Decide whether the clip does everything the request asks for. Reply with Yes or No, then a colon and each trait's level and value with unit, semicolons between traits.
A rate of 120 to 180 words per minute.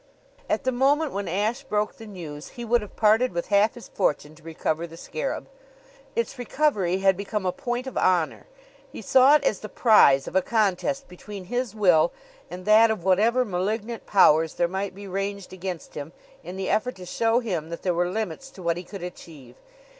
No: average, 200 wpm